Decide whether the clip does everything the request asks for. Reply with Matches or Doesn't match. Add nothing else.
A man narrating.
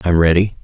Matches